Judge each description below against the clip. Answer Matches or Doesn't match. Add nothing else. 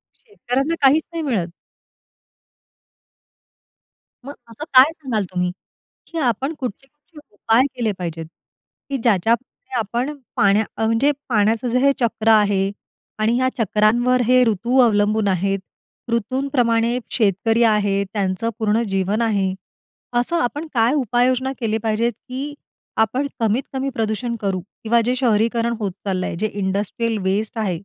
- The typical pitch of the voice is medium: Doesn't match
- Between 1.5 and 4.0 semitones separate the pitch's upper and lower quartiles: Matches